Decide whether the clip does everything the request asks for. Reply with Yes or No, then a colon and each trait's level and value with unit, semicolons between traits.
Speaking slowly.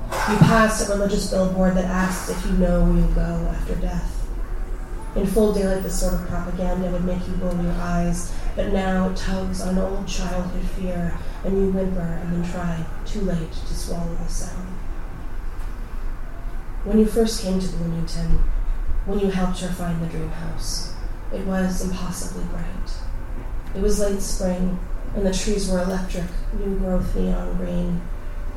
No: average, 165 wpm